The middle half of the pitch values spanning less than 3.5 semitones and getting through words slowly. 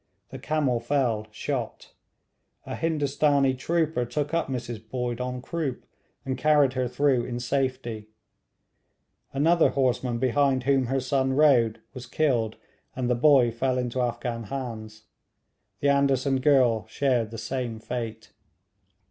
Yes: average, 2.7 semitones; slow, 130 wpm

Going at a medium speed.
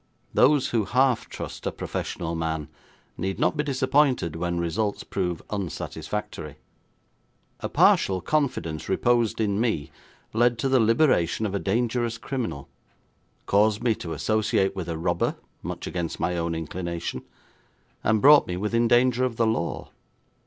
Yes: average, 145 wpm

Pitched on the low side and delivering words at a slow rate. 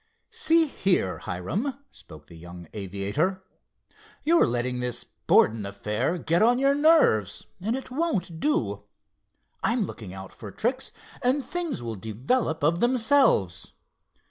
No: medium, 165 Hz; slow, 130 wpm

